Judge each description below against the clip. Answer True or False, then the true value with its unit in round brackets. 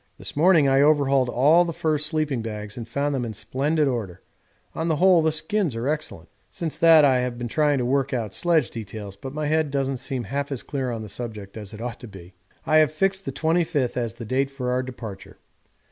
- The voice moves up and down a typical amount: True (4.7 semitones)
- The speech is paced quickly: True (225 wpm)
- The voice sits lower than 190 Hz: True (135 Hz)